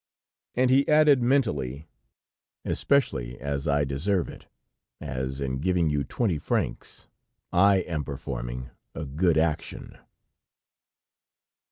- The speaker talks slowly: Yes, slow, 110 wpm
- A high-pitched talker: No, very low, 75 Hz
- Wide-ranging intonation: Yes, wide, 6.4 semitones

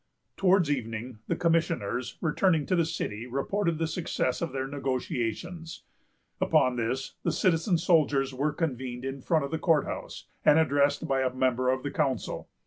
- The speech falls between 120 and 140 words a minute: No, average, 165 wpm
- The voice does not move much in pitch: No, average, 4.3 semitones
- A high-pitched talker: No, medium, 140 Hz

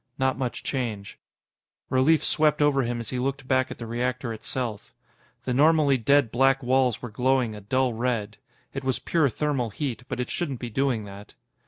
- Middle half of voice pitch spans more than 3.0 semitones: No, narrow, 2.5 semitones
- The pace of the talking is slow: No, average, 185 wpm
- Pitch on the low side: Yes, low, 130 Hz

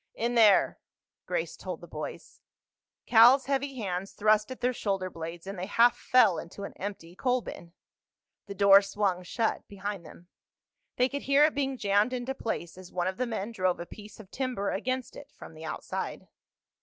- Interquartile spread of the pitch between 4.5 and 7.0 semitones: Yes, average, 5.0 semitones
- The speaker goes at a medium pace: Yes, average, 180 wpm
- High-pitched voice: Yes, high, 205 Hz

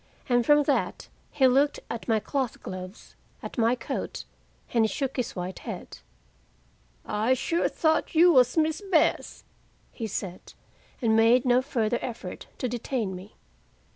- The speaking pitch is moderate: No, high, 245 Hz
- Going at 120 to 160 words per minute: Yes, average, 150 wpm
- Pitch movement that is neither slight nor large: Yes, average, 3.9 semitones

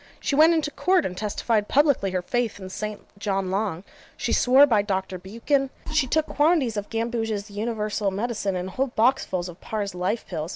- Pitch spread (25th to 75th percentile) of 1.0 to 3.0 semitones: No, average, 5.0 semitones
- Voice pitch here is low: No, high, 215 Hz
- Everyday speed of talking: Yes, average, 180 wpm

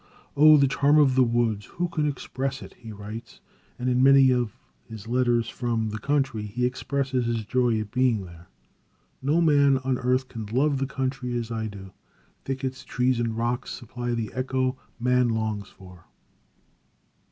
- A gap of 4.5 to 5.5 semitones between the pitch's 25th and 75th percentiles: No, average, 2.9 semitones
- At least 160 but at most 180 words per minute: Yes, average, 170 wpm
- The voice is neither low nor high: No, low, 125 Hz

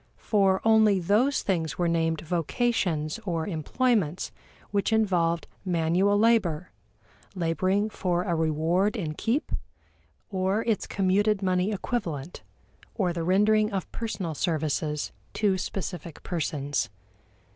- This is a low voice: No, medium, 185 Hz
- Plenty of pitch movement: No, average, 4.0 semitones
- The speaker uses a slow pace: Yes, slow, 115 wpm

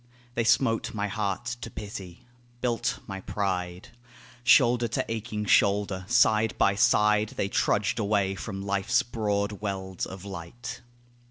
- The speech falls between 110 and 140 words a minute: Yes, slow, 135 wpm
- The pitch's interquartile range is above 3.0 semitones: No, narrow, 2.5 semitones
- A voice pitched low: Yes, low, 105 Hz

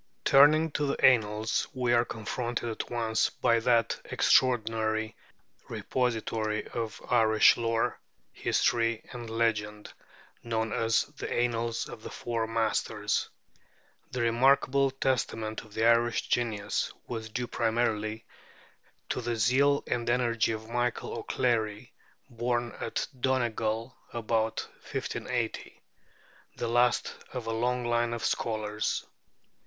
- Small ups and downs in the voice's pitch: Yes, narrow, 1.6 semitones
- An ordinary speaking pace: No, slow, 115 wpm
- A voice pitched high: No, low, 115 Hz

